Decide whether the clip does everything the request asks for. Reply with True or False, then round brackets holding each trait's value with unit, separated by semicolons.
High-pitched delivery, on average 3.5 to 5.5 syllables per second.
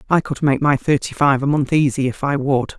False (140 Hz; 5.4 syllables/s)